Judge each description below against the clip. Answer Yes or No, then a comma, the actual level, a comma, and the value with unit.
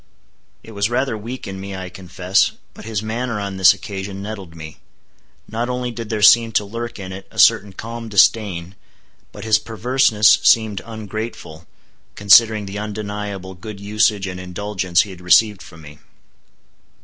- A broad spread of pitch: No, average, 2.8 semitones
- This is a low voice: Yes, low, 105 Hz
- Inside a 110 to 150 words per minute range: No, average, 160 wpm